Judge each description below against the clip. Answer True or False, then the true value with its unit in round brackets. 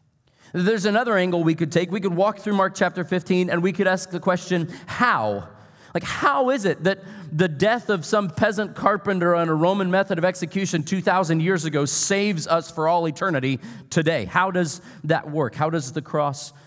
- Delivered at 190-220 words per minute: True (195 wpm)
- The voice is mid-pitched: True (180 Hz)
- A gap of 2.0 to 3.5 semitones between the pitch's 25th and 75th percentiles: True (3.2 semitones)